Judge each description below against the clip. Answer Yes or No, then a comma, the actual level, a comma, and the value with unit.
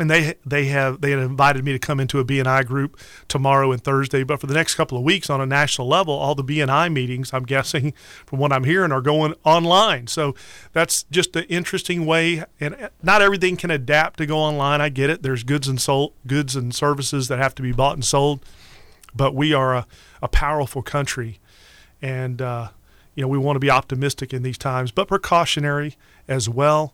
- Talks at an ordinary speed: No, fast, 210 wpm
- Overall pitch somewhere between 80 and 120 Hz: No, medium, 140 Hz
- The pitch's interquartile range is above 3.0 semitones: No, narrow, 2.6 semitones